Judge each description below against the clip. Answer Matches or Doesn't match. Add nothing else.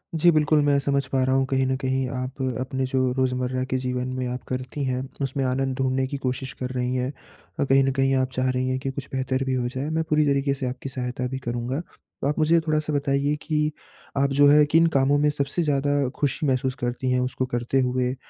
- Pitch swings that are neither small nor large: Doesn't match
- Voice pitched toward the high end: Doesn't match